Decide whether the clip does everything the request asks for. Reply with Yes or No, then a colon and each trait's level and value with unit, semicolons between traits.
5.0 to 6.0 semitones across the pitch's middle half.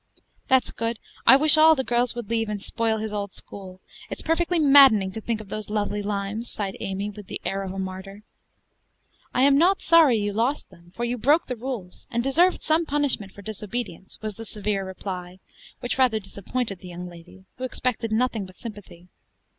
No: average, 4.5 semitones